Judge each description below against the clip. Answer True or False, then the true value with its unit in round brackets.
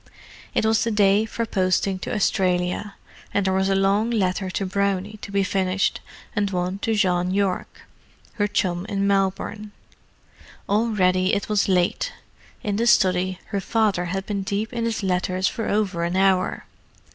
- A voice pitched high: True (195 Hz)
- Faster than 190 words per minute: False (165 wpm)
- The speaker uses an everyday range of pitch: False (2.0 semitones)